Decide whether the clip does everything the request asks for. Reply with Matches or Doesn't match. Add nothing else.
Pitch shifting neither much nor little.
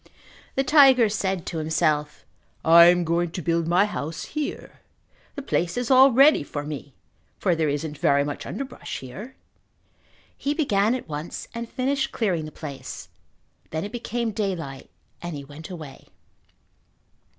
Doesn't match